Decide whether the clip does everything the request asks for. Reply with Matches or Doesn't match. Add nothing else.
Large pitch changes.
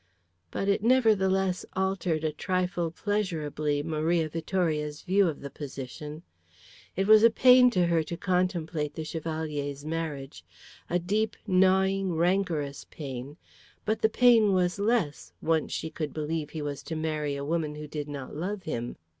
Doesn't match